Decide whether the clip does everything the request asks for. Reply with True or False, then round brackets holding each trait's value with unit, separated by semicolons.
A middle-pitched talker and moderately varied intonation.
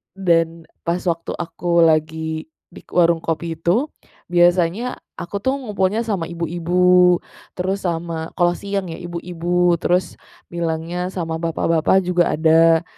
False (170 Hz; 1.6 semitones)